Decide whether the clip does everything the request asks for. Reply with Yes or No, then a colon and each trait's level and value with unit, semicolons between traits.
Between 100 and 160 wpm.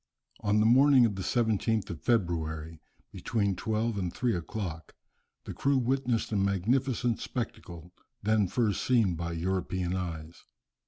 Yes: average, 140 wpm